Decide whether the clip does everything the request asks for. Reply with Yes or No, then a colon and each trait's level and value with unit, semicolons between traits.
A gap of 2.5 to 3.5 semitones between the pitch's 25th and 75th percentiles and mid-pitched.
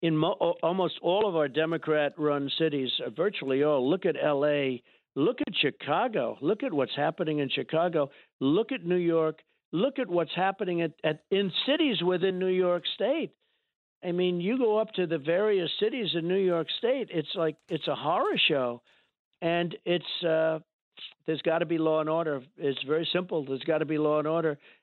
Yes: average, 2.9 semitones; medium, 165 Hz